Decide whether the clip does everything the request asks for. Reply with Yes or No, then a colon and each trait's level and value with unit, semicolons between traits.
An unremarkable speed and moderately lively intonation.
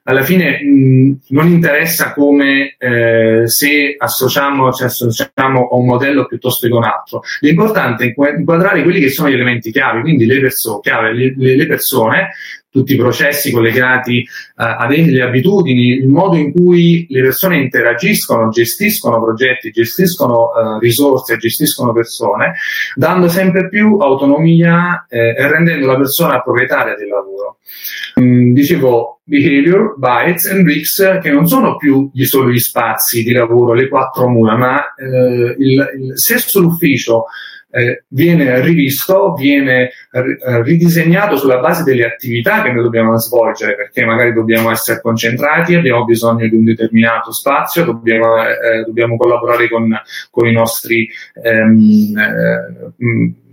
Yes: average, 145 wpm; average, 4.6 semitones